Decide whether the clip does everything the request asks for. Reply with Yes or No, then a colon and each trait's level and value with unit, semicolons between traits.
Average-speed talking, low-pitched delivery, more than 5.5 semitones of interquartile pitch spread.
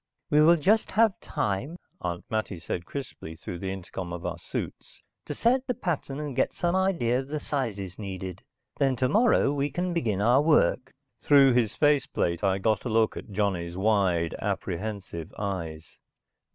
Yes: average, 170 wpm; low, 110 Hz; wide, 7.6 semitones